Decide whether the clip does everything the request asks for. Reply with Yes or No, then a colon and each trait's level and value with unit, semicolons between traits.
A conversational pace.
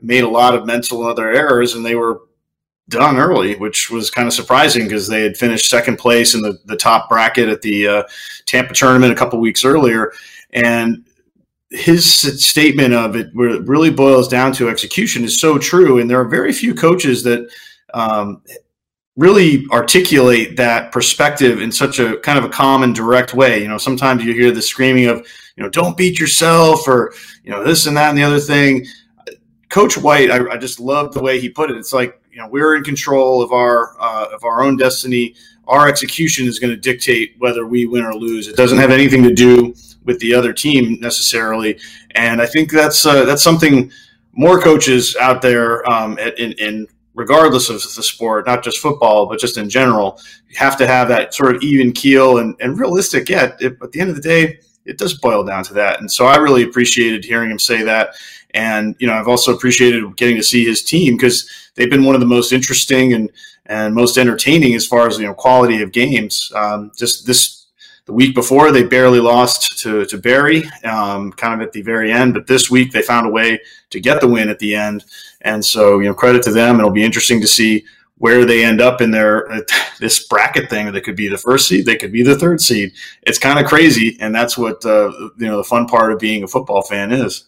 No: fast, 220 wpm